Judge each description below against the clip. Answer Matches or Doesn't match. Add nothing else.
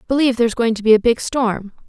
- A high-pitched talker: Matches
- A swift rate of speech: Matches